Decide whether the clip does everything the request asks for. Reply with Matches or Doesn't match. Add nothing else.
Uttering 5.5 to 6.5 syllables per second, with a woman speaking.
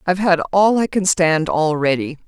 Doesn't match